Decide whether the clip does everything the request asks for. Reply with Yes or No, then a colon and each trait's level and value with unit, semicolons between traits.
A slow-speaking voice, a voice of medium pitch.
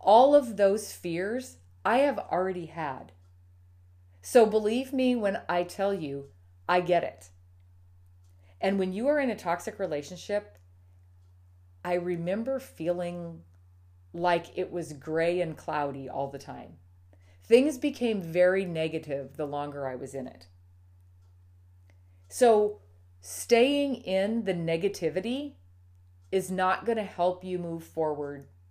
Yes: slow, 130 wpm; medium, 160 Hz